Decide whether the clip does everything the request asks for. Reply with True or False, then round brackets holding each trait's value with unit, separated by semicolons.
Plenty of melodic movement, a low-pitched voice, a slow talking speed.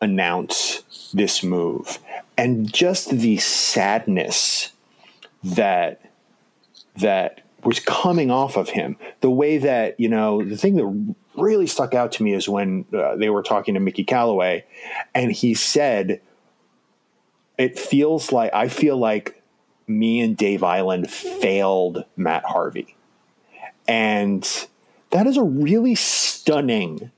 True (6.8 semitones; 115 Hz; 130 wpm)